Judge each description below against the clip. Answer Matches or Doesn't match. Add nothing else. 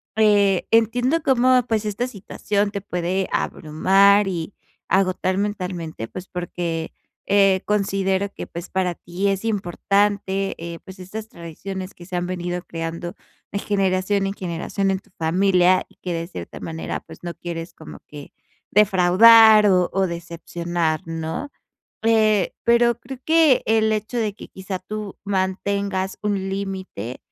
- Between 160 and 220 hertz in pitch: Matches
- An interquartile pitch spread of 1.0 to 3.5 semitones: Matches